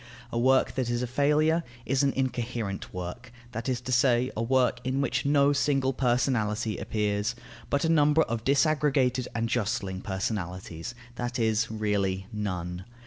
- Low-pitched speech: Yes, low, 120 Hz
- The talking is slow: No, average, 155 wpm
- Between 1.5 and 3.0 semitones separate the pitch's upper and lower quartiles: No, average, 4.1 semitones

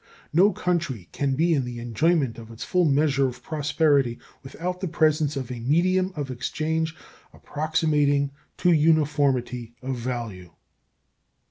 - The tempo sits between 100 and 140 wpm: Yes, slow, 135 wpm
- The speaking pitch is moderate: Yes, medium, 145 Hz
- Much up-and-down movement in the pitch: No, average, 4.3 semitones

